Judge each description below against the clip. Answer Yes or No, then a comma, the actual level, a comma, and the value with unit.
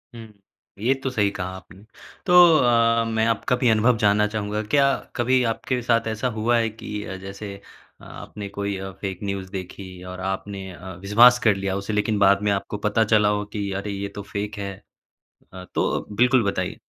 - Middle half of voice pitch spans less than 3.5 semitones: Yes, narrow, 2.6 semitones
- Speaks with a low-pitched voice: Yes, low, 105 Hz